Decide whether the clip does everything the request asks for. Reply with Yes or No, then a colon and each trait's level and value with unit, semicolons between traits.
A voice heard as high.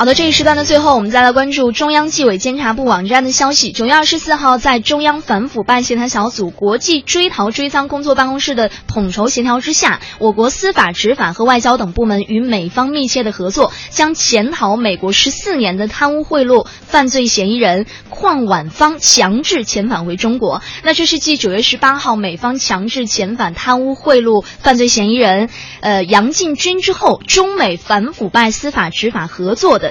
Yes: high, 245 Hz